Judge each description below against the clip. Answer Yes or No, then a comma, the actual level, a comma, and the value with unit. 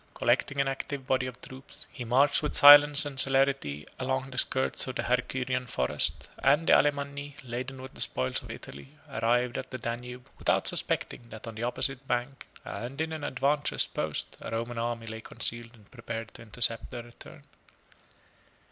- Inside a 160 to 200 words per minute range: Yes, average, 175 wpm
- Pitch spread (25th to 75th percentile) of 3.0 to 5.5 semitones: No, narrow, 2.6 semitones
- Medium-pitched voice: No, low, 125 Hz